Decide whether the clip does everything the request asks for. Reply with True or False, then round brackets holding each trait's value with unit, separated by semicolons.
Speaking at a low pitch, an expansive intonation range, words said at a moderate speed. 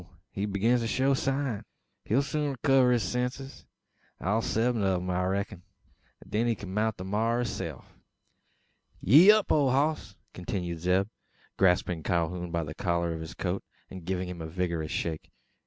True (100 Hz; 5.7 semitones; 170 wpm)